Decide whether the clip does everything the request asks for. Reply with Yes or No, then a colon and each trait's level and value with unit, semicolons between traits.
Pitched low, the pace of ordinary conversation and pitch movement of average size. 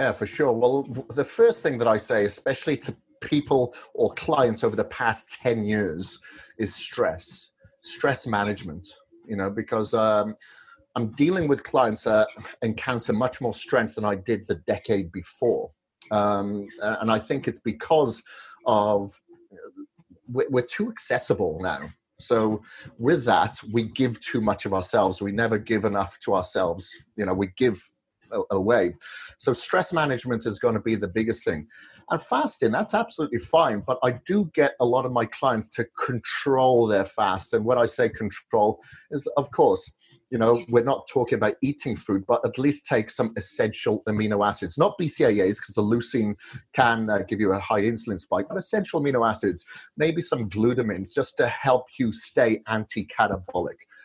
Yes: low, 115 Hz; average, 165 wpm; average, 4.6 semitones